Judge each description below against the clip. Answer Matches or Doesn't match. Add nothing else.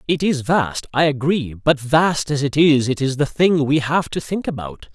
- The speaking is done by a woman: Doesn't match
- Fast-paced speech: Matches